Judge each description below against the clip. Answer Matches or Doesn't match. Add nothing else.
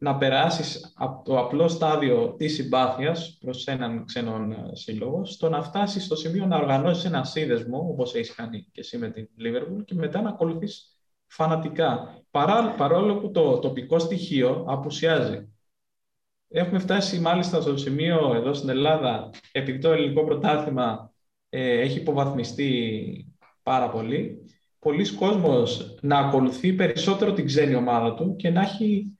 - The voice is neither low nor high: Matches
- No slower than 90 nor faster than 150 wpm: Matches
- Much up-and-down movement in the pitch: Doesn't match